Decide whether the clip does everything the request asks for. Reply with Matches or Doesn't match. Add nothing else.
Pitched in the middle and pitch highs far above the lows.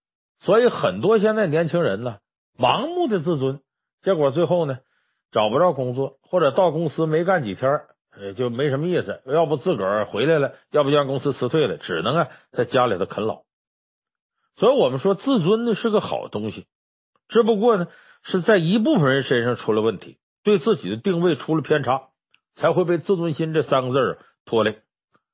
Matches